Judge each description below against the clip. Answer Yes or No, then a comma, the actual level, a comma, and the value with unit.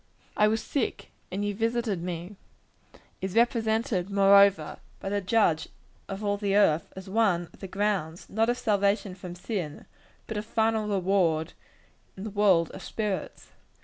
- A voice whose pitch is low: No, high, 200 Hz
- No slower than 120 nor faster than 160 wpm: Yes, average, 155 wpm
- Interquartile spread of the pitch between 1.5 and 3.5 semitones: Yes, average, 2.9 semitones